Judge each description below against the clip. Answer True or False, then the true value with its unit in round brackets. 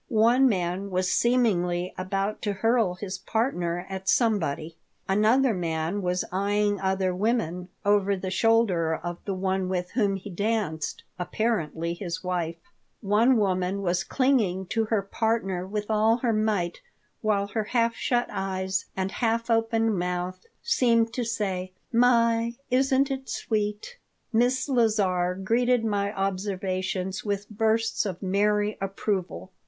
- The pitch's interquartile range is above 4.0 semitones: False (3.6 semitones)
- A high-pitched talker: True (200 Hz)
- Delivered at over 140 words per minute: False (135 wpm)